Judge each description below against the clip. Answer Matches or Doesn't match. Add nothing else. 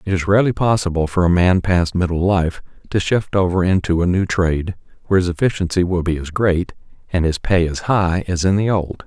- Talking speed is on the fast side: Matches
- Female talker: Doesn't match